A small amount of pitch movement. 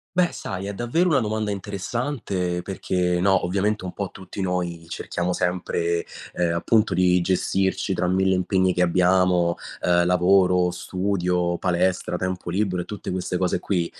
Yes: narrow, 1.7 semitones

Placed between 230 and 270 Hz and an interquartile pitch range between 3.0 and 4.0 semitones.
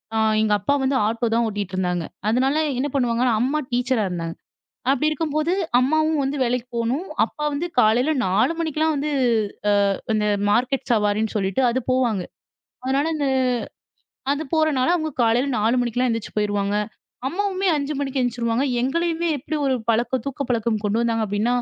No: very high, 250 Hz; average, 4.4 semitones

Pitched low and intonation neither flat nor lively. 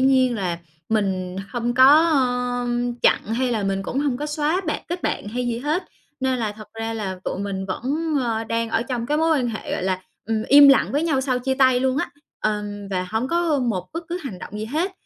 No: high, 245 Hz; average, 4.5 semitones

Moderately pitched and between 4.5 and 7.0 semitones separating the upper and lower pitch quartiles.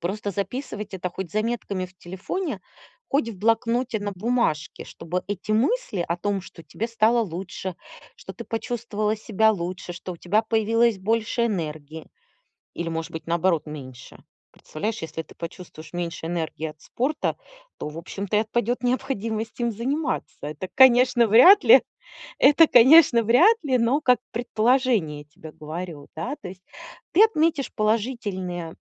No: high, 210 Hz; wide, 5.5 semitones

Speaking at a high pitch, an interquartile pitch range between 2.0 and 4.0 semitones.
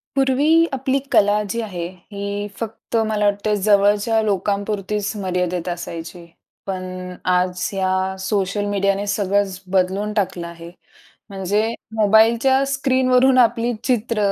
Yes: high, 205 Hz; average, 3.1 semitones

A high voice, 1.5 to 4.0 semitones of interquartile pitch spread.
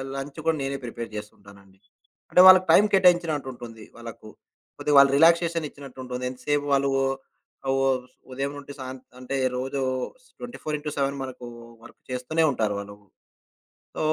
No: low, 135 Hz; average, 3.4 semitones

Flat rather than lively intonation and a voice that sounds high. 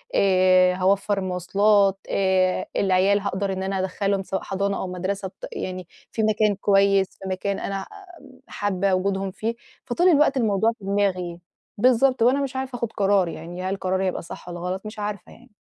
Yes: narrow, 1.9 semitones; high, 195 Hz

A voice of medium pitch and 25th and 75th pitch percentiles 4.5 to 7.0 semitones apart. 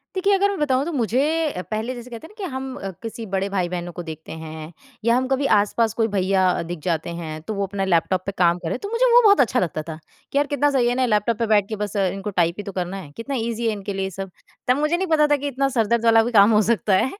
No: high, 215 Hz; wide, 5.6 semitones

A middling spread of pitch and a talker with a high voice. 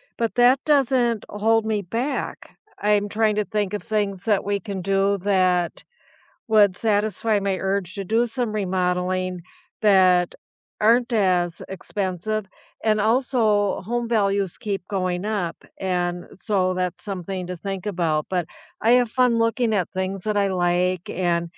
Yes: average, 3.0 semitones; high, 200 Hz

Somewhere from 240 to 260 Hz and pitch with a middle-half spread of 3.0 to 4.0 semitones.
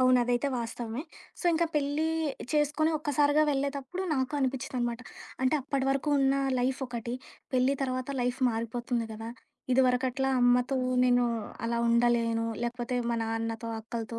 No: very high, 250 Hz; narrow, 2.5 semitones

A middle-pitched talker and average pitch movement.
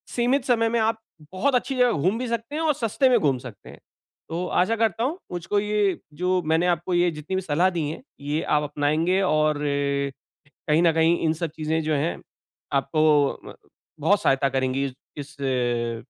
No: medium, 165 Hz; wide, 6.4 semitones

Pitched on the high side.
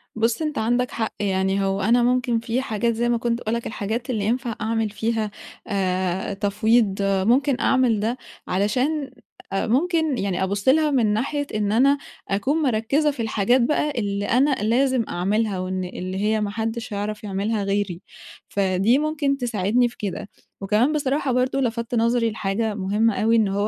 Yes: high, 225 Hz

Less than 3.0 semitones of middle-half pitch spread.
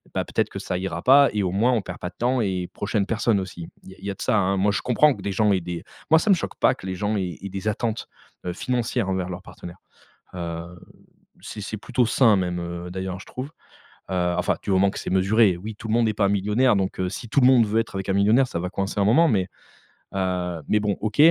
No: average, 3.3 semitones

